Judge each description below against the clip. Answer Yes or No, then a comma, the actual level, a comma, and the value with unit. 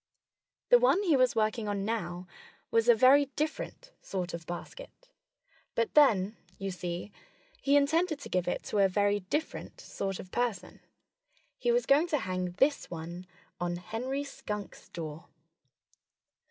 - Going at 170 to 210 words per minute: No, average, 150 wpm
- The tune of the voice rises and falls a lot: Yes, wide, 7.7 semitones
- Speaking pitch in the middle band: No, high, 215 Hz